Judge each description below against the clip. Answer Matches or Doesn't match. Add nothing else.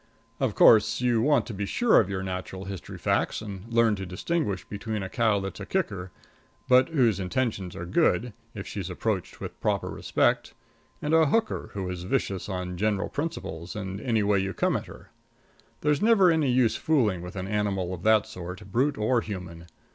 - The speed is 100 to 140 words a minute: Doesn't match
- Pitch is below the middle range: Matches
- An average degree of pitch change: Matches